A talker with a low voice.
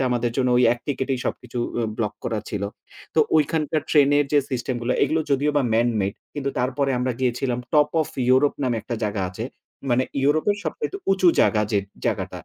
Yes: low, 130 Hz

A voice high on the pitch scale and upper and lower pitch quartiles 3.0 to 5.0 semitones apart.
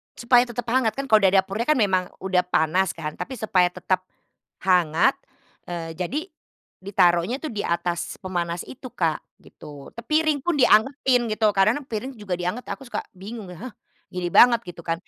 No: high, 195 Hz; wide, 5.4 semitones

